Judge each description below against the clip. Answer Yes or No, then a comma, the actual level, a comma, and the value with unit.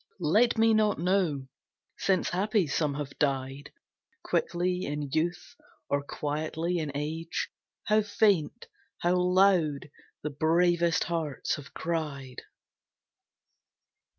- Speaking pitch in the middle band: Yes, medium, 165 Hz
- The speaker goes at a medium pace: No, slow, 105 wpm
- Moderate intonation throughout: Yes, average, 3.7 semitones